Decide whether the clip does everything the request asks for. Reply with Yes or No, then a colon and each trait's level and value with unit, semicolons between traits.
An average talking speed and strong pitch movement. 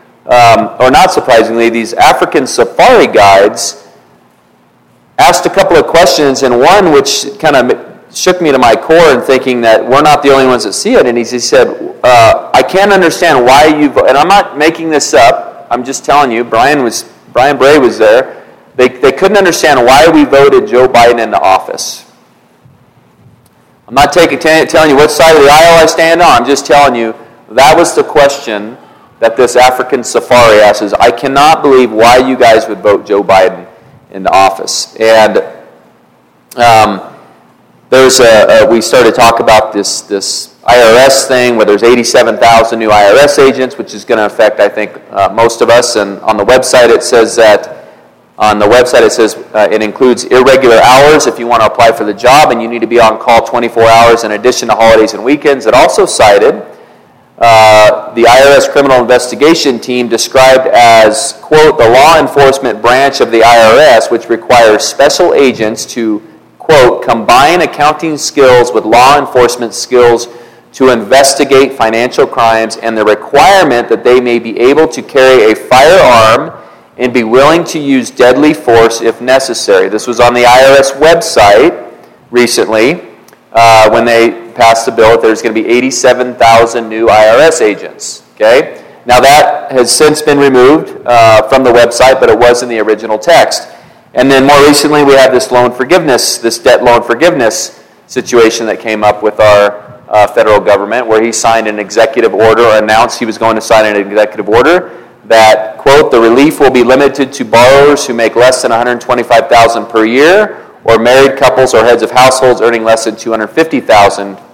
No: average, 180 wpm; average, 3.5 semitones